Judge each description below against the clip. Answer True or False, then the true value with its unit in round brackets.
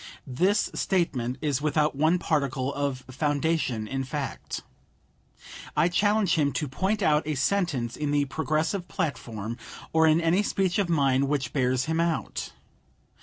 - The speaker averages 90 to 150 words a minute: True (145 wpm)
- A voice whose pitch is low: False (150 Hz)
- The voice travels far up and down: False (4.0 semitones)